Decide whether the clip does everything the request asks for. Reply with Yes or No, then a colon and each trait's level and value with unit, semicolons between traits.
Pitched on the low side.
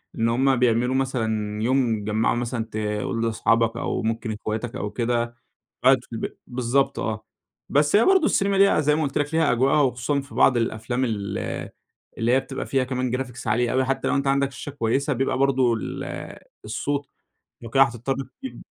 Yes: low, 125 Hz